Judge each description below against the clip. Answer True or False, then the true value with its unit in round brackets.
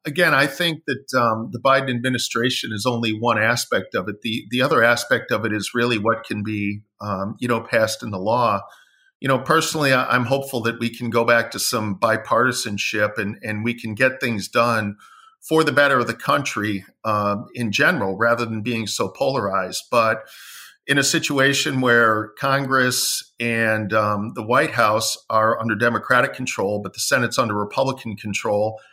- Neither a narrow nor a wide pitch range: True (3.4 semitones)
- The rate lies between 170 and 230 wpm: True (180 wpm)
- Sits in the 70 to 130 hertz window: True (115 Hz)